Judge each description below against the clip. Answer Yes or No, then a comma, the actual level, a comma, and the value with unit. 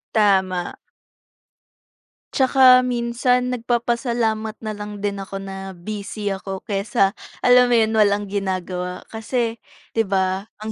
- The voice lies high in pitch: Yes, high, 210 Hz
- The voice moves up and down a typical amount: Yes, average, 3.3 semitones